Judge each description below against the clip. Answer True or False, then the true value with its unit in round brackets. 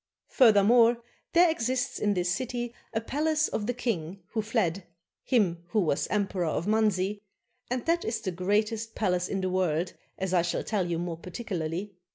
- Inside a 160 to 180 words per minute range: True (175 wpm)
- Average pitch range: True (4.6 semitones)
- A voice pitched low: False (205 Hz)